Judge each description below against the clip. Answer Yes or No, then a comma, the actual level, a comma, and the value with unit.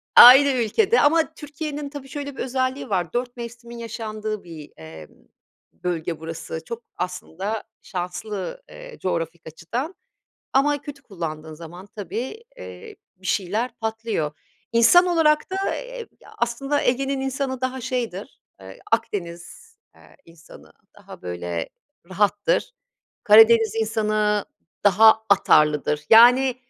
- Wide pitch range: Yes, wide, 7.0 semitones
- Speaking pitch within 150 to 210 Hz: No, high, 225 Hz